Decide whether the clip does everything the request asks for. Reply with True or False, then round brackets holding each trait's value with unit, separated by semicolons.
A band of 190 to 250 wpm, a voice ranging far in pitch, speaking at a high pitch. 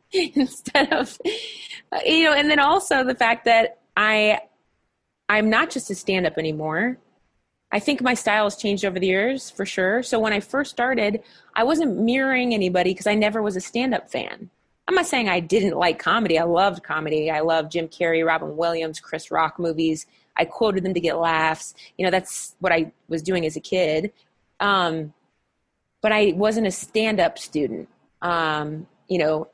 False (180 wpm; 6.2 semitones; 205 Hz)